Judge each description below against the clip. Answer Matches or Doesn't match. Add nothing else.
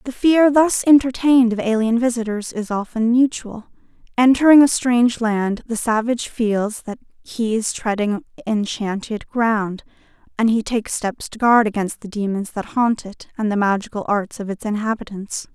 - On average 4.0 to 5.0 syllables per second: Matches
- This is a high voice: Matches